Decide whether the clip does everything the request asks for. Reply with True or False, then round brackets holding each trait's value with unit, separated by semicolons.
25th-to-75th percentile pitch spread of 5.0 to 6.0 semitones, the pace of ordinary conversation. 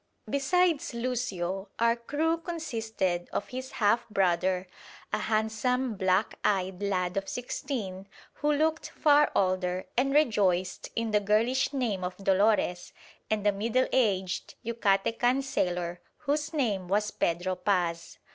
False (5.4 semitones; 130 wpm)